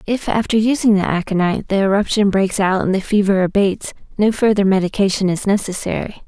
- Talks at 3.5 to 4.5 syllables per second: No, 5.9 syllables/s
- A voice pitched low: No, high, 200 Hz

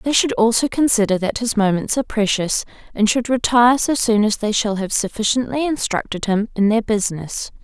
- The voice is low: No, high, 220 Hz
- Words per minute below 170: No, average, 190 wpm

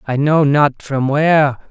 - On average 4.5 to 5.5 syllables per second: No, 4.1 syllables/s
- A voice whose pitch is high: No, medium, 145 Hz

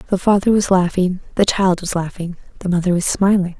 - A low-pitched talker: No, medium, 185 Hz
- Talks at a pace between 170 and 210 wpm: Yes, average, 200 wpm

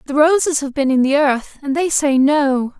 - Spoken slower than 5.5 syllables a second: Yes, 4.6 syllables/s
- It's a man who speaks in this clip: No, female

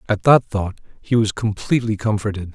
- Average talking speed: Yes, average, 165 wpm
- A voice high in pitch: No, low, 105 Hz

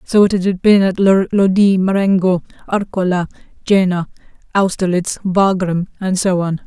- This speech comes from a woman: Yes, female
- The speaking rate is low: Yes, slow, 125 wpm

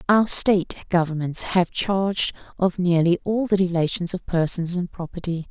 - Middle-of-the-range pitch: Yes, medium, 180 Hz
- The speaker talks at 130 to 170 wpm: Yes, average, 155 wpm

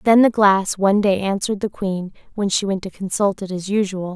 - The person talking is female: Yes, female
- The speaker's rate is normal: No, fast, 230 wpm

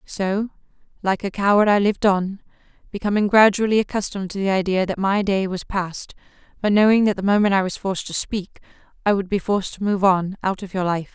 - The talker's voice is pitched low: No, high, 195 Hz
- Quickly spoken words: Yes, fast, 210 wpm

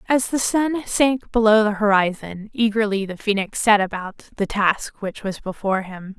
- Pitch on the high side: Yes, high, 210 Hz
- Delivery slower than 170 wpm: No, average, 175 wpm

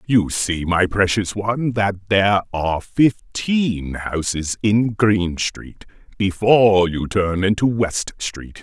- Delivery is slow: Yes, slow, 130 wpm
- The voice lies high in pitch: No, low, 100 Hz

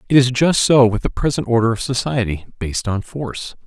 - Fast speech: Yes, fast, 215 wpm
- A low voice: Yes, low, 120 Hz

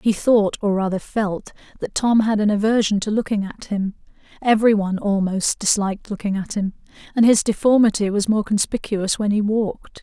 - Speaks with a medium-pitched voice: No, high, 210 Hz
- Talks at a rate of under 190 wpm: Yes, average, 180 wpm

